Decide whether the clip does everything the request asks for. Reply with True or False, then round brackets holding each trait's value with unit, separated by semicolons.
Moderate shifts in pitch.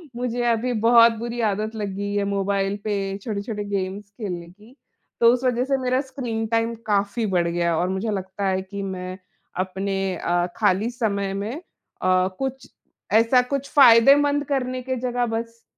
True (3.7 semitones)